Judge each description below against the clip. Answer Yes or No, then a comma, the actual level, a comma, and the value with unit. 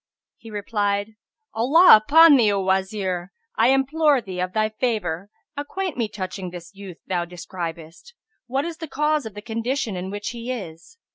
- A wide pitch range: Yes, wide, 6.2 semitones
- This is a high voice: Yes, high, 215 Hz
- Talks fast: No, average, 165 wpm